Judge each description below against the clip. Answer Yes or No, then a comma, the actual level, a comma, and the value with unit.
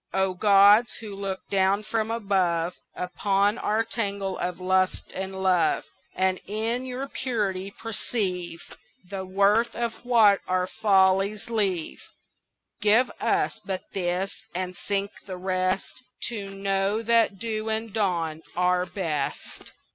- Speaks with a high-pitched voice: Yes, high, 195 Hz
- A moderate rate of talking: No, slow, 125 wpm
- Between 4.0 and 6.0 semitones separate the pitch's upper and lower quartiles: No, average, 2.7 semitones